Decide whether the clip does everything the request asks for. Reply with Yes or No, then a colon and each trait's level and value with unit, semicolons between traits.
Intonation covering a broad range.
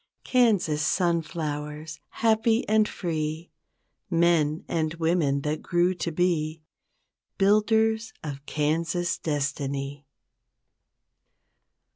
No: average, 3.4 semitones